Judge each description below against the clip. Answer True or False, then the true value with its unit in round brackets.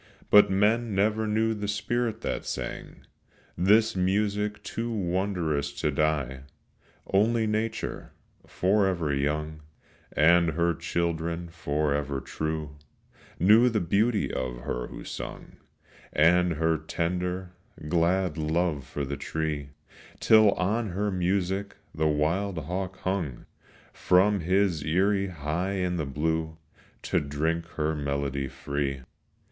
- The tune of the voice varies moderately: True (4.6 semitones)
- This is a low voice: True (85 Hz)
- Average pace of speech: False (120 wpm)